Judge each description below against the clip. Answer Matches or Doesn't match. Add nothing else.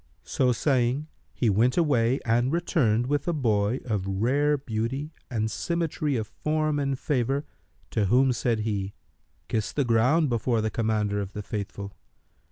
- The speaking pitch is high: Doesn't match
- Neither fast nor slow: Matches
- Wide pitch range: Doesn't match